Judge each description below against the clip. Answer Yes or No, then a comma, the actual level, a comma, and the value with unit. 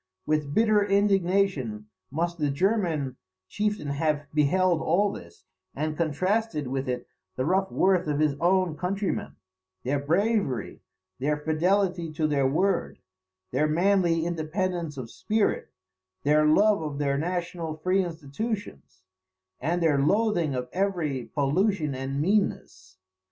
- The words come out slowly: Yes, slow, 125 wpm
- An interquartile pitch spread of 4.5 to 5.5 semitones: Yes, average, 4.9 semitones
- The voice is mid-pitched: Yes, medium, 160 Hz